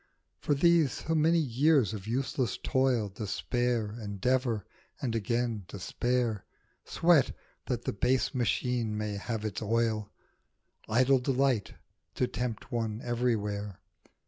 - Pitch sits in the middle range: No, low, 120 Hz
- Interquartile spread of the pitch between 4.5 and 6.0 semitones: No, average, 3.5 semitones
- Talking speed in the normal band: No, slow, 120 wpm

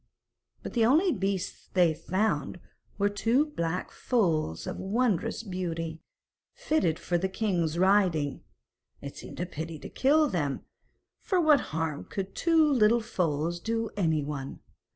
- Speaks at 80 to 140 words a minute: Yes, slow, 135 wpm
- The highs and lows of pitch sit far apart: Yes, wide, 5.8 semitones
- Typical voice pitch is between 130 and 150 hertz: No, medium, 185 Hz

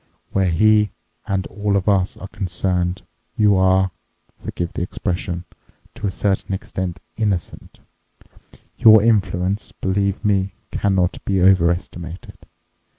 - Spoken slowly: Yes, slow, 105 wpm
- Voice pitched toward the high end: No, very low, 95 Hz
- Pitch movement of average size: No, narrow, 2.1 semitones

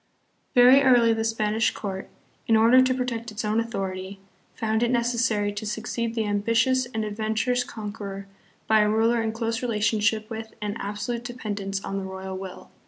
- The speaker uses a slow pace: No, average, 170 wpm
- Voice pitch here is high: Yes, high, 220 Hz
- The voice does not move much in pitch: Yes, narrow, 2.2 semitones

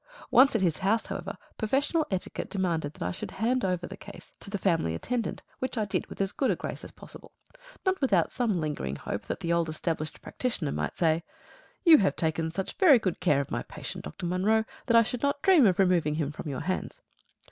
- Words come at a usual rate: No, fast, 220 wpm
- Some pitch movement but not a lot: No, wide, 6.5 semitones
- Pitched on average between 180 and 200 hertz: Yes, high, 190 Hz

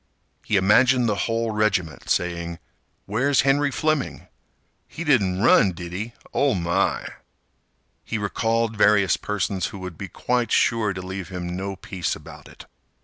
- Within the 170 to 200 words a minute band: No, average, 145 wpm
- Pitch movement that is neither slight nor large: Yes, average, 4.0 semitones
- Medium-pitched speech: No, low, 105 Hz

